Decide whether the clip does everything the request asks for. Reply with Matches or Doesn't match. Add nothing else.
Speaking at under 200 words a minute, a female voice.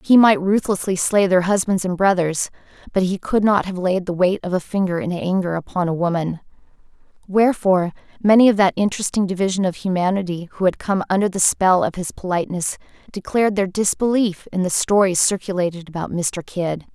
Matches